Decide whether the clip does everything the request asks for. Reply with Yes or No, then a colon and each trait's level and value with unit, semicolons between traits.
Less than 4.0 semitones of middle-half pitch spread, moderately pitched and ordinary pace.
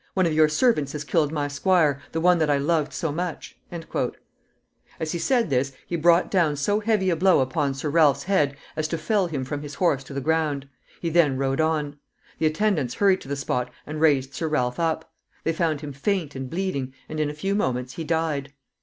No: average, 3.3 semitones; medium, 155 Hz; fast, 215 wpm